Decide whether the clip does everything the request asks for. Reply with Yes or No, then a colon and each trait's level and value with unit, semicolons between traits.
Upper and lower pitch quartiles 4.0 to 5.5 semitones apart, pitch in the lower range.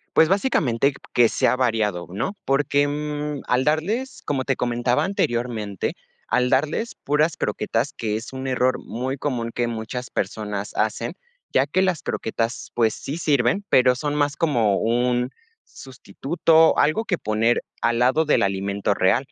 Yes: average, 4.4 semitones; low, 125 Hz